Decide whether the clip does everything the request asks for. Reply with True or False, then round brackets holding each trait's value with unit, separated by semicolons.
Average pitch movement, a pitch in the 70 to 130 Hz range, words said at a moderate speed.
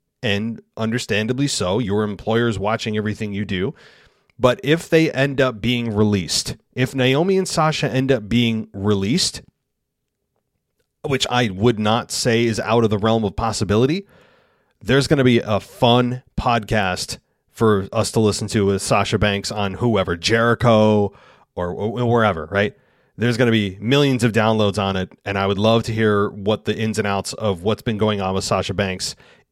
True (3.0 semitones; 110 Hz; 175 wpm)